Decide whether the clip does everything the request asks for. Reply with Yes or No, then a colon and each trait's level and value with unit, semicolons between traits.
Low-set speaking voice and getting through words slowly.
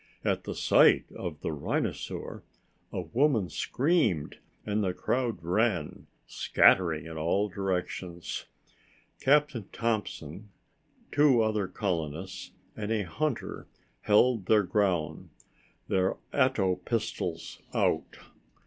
Yes: low, 100 Hz; slow, 105 wpm